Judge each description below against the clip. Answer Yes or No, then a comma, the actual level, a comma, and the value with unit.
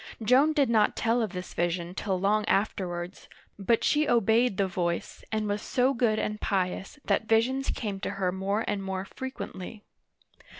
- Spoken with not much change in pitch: No, average, 3.6 semitones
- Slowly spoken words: No, average, 170 wpm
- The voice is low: No, high, 210 Hz